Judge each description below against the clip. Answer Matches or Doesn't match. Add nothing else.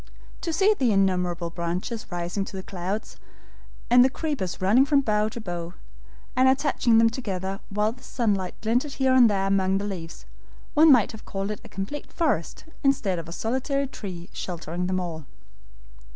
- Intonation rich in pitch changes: Matches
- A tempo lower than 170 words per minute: Doesn't match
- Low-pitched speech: Doesn't match